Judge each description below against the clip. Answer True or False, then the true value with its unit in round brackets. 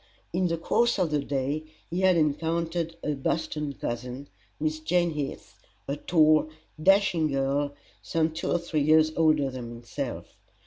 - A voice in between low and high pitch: True (155 Hz)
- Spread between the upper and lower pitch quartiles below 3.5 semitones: True (2.8 semitones)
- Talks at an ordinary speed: True (150 wpm)